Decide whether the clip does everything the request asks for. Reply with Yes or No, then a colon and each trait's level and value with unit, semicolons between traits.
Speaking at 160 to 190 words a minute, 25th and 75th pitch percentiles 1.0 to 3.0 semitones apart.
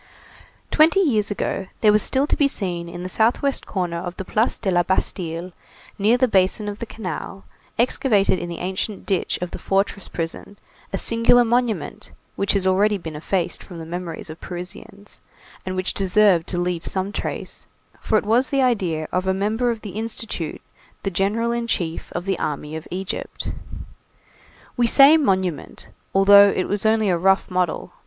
No: average, 180 wpm; average, 3.7 semitones